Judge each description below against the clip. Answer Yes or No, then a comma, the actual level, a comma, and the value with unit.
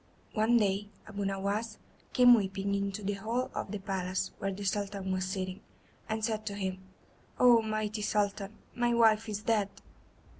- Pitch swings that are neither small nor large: No, narrow, 2.0 semitones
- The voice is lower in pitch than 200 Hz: No, high, 205 Hz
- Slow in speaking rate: No, average, 160 wpm